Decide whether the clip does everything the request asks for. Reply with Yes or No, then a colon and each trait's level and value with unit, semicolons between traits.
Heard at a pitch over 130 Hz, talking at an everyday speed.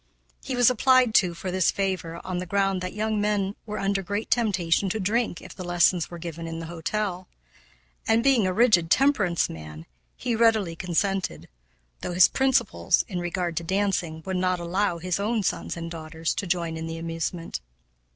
Yes: medium, 185 Hz; average, 185 wpm